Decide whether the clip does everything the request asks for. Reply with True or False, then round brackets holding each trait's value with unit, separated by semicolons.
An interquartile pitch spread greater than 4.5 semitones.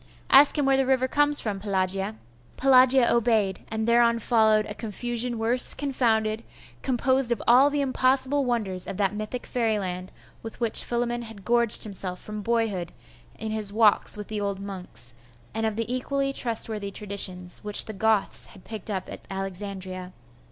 False (3.4 semitones)